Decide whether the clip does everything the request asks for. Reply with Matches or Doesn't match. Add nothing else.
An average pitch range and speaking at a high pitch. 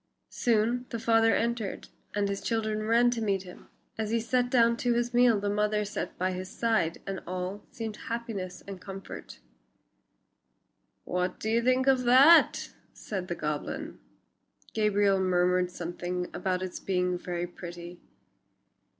Matches